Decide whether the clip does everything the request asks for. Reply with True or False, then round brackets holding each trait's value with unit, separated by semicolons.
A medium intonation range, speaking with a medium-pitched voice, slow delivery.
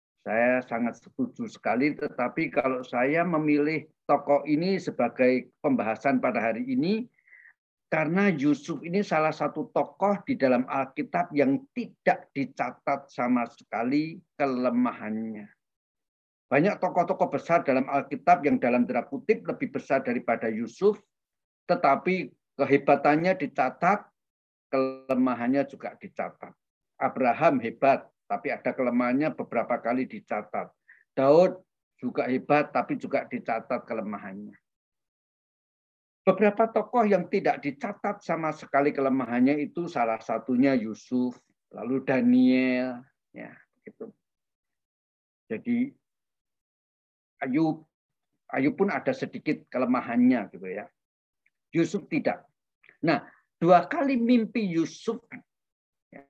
False (6.6 semitones; 145 Hz; 100 wpm)